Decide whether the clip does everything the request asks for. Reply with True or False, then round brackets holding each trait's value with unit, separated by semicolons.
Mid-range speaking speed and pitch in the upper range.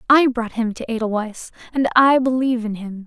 True (195 wpm; 235 Hz)